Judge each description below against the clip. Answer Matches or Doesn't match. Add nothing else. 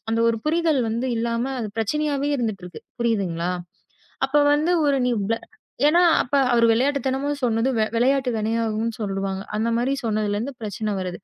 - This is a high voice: Matches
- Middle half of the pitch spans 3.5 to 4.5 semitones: Matches